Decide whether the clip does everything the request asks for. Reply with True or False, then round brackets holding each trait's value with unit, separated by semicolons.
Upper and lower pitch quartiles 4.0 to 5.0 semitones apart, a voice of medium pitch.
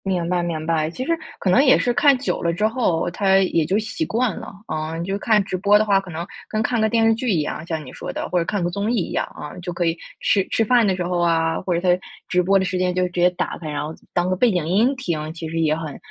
True (4.3 semitones; 180 Hz)